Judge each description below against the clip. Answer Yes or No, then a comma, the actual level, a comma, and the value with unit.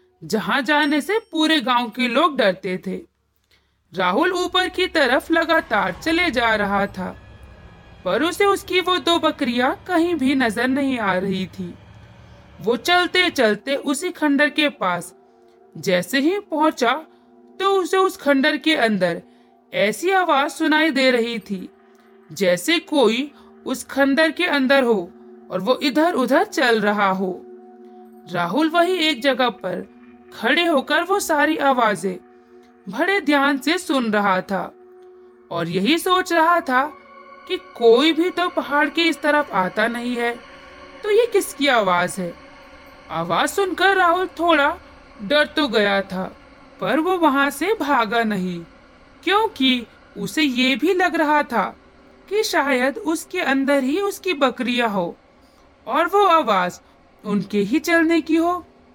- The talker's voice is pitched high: Yes, very high, 280 Hz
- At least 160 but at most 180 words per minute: No, average, 140 wpm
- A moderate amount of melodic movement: No, wide, 7.8 semitones